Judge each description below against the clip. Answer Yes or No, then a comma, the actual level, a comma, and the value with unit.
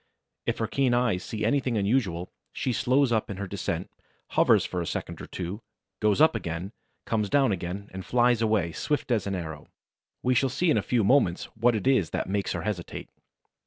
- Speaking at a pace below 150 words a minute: No, average, 200 wpm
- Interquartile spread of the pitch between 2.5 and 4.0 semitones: No, average, 5.1 semitones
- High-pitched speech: No, low, 105 Hz